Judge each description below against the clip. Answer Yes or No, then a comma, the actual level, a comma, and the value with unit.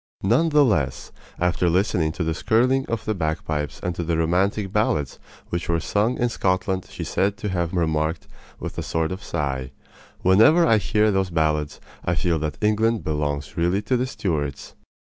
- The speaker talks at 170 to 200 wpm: Yes, average, 185 wpm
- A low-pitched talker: Yes, very low, 90 Hz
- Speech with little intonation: No, average, 5.1 semitones